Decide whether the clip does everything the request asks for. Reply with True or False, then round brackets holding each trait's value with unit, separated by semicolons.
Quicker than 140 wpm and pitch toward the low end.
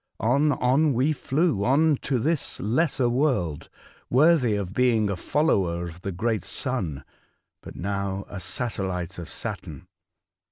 False (135 wpm; 120 Hz)